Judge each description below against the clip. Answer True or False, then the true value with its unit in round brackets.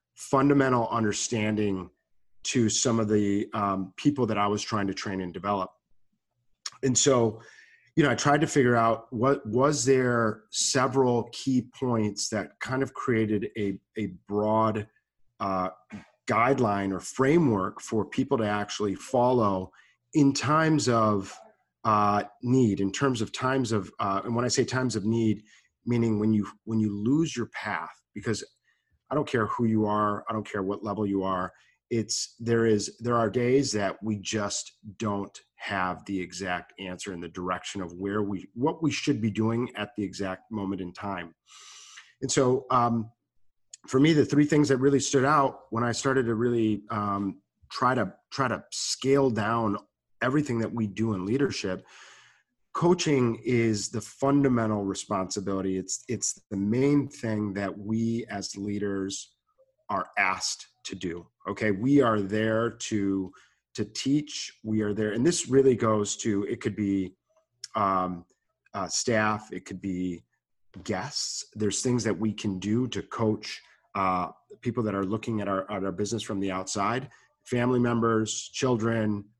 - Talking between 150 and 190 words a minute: True (160 wpm)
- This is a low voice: True (110 Hz)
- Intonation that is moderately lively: True (3.5 semitones)